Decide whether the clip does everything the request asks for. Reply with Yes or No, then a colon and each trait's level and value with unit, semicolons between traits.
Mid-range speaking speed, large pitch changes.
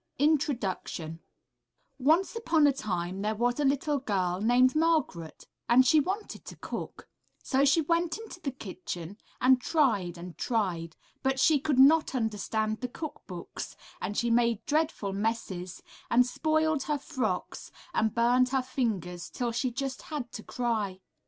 Yes: average, 150 wpm; wide, 6.1 semitones